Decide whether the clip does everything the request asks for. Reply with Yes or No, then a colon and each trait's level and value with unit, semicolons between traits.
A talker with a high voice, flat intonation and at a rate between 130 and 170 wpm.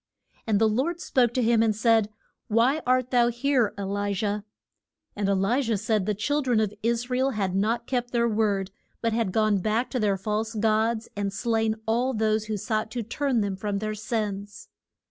No: high, 220 Hz; narrow, 2.3 semitones; fast, 205 wpm